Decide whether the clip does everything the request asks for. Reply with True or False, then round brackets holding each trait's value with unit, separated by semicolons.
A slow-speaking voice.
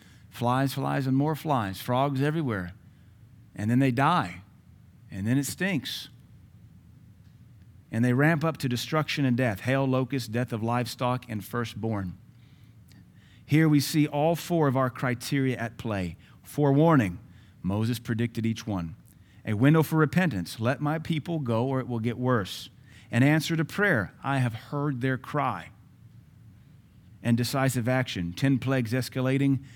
False (145 wpm)